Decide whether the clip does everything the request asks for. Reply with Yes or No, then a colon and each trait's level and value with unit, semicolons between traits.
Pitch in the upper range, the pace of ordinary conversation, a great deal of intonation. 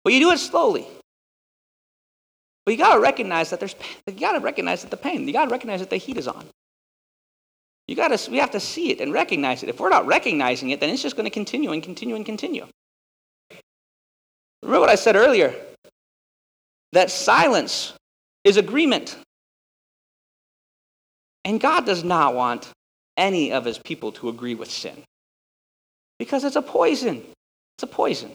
Yes: high, 220 Hz; average, 165 wpm; wide, 8.6 semitones